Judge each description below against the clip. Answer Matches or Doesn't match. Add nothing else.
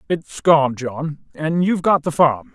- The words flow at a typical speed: Matches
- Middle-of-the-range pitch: Matches